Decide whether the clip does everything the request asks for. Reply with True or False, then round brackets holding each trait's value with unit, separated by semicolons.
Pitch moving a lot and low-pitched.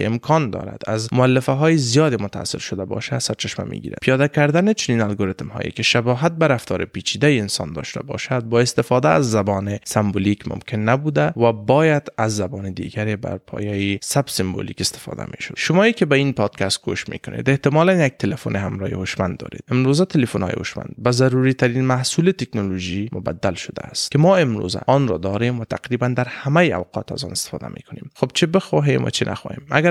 True (5.8 semitones; 125 Hz)